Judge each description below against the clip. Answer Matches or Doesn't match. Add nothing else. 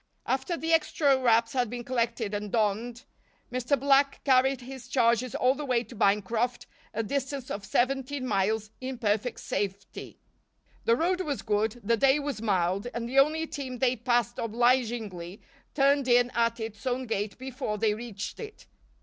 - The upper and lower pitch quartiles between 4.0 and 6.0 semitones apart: Doesn't match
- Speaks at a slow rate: Doesn't match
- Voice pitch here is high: Matches